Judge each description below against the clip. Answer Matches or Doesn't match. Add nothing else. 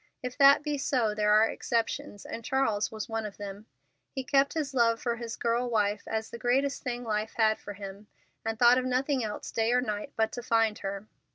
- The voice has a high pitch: Matches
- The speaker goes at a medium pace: Doesn't match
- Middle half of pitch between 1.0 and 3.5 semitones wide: Matches